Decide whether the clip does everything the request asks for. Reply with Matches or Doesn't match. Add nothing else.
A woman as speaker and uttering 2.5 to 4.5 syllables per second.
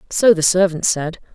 Doesn't match